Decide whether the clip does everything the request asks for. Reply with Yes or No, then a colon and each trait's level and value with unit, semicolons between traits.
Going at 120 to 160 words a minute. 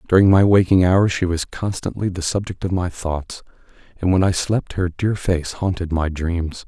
No: average, 200 wpm